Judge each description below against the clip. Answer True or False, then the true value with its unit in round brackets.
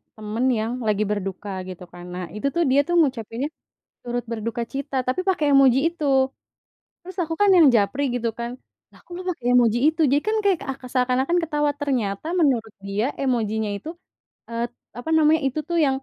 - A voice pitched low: False (250 Hz)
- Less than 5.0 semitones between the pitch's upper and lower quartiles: False (5.4 semitones)